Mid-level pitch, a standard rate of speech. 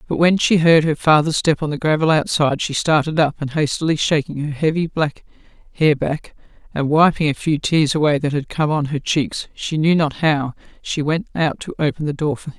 No: medium, 155 Hz; fast, 225 wpm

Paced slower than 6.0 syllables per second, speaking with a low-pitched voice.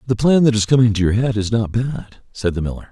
No: 6.1 syllables/s; low, 115 Hz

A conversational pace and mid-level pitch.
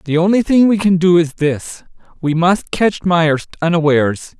Yes: average, 165 wpm; medium, 170 Hz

